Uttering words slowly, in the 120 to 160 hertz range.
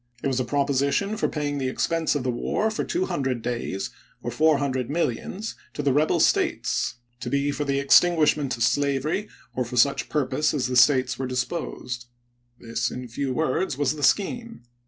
No: average, 185 wpm; medium, 140 Hz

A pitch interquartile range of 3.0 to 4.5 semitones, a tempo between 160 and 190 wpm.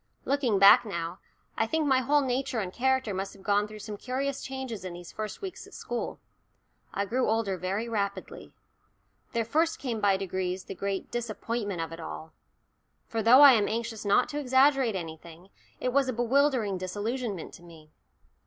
No: average, 5.0 semitones; average, 180 wpm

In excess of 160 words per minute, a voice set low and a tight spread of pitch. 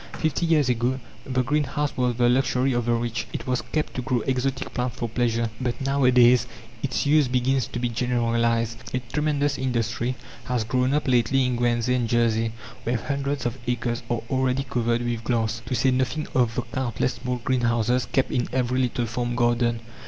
Yes: average, 185 wpm; low, 125 Hz; narrow, 1.8 semitones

